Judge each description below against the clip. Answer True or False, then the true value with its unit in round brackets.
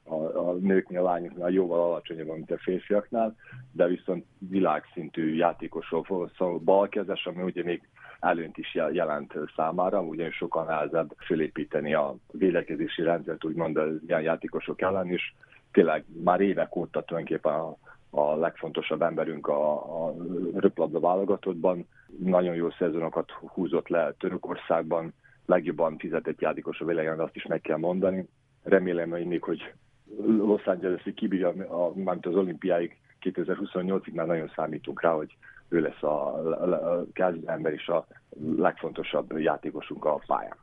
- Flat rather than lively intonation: True (1.8 semitones)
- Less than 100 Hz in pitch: True (90 Hz)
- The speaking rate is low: False (135 wpm)